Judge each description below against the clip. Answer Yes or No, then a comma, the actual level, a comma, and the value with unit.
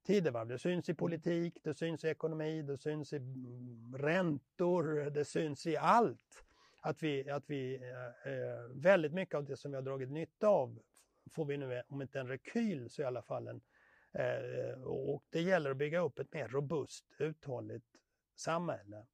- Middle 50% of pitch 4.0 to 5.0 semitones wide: No, average, 3.6 semitones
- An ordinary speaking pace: Yes, average, 170 wpm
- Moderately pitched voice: Yes, medium, 145 Hz